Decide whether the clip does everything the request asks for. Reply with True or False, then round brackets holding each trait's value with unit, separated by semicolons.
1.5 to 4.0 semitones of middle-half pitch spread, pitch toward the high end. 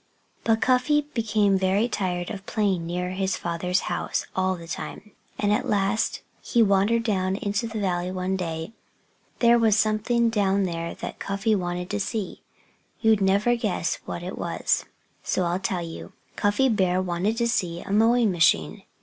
True (3.5 semitones; 195 Hz)